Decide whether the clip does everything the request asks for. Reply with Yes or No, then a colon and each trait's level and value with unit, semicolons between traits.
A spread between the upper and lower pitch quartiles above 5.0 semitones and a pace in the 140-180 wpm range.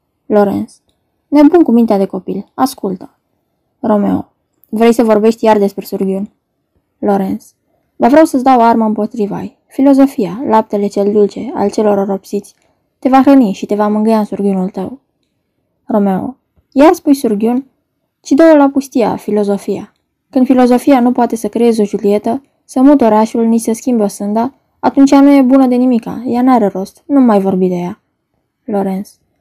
No: average, 4.5 semitones; average, 160 wpm